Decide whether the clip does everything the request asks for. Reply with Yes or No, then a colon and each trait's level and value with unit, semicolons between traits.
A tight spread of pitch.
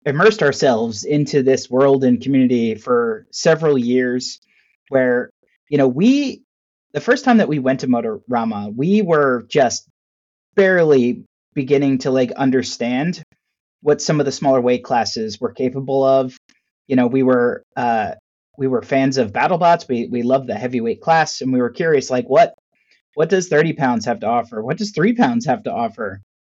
No: average, 4.0 semitones